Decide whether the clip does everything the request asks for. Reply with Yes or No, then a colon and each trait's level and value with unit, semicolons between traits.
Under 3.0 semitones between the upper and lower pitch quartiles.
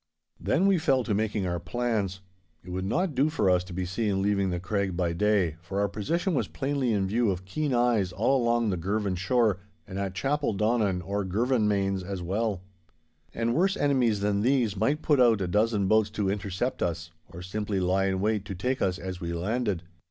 No: average, 4.2 semitones